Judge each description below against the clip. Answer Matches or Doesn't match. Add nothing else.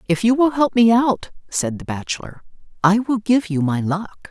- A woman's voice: Matches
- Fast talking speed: Matches